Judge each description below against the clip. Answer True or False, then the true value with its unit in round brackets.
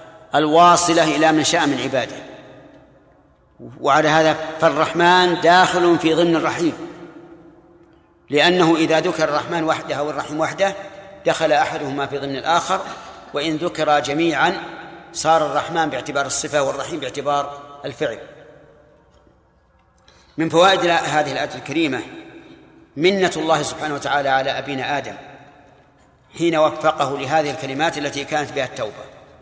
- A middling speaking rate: True (110 wpm)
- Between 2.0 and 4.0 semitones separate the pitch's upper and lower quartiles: True (2.8 semitones)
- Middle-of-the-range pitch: True (155 Hz)